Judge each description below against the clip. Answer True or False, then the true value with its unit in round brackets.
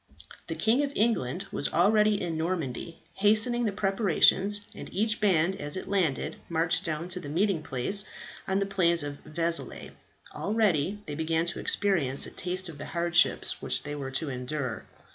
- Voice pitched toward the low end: False (175 Hz)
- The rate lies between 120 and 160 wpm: False (170 wpm)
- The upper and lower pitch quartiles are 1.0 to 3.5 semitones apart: False (4.6 semitones)